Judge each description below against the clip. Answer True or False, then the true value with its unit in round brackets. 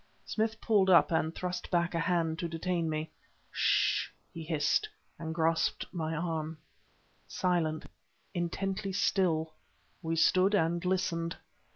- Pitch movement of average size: False (2.3 semitones)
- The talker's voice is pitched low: False (170 Hz)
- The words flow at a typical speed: False (130 wpm)